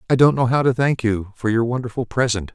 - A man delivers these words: Yes, male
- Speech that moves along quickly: Yes, fast, 260 wpm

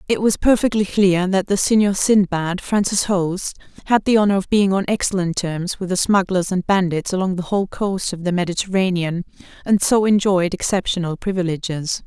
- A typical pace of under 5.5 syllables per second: Yes, 5.1 syllables/s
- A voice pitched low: No, high, 190 Hz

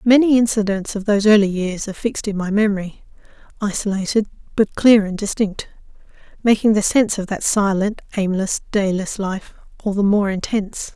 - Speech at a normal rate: Yes, average, 160 wpm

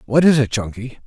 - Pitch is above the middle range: No, low, 125 Hz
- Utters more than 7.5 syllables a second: No, 5.7 syllables/s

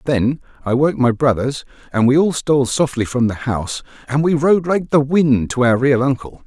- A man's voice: Yes, male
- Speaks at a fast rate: Yes, fast, 215 wpm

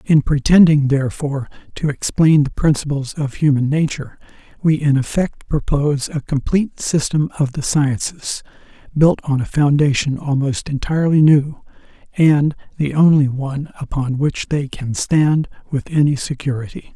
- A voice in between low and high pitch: Yes, medium, 145 Hz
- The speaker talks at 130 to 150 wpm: Yes, average, 140 wpm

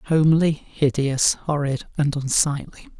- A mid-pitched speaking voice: Yes, medium, 145 Hz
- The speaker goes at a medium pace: No, slow, 100 wpm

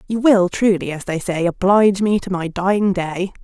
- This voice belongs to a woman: Yes, female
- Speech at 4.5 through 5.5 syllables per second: Yes, 5.1 syllables/s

